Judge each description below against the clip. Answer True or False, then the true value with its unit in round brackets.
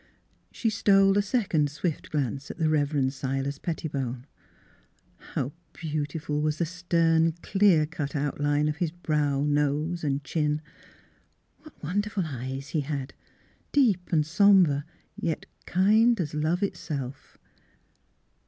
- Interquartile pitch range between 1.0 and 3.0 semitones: False (3.7 semitones)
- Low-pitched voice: False (155 Hz)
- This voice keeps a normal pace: False (125 wpm)